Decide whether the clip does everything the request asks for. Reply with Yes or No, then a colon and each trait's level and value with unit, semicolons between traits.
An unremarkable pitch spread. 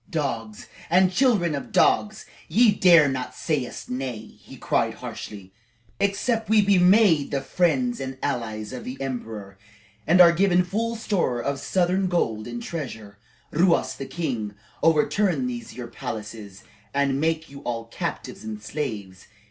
No: wide, 8.3 semitones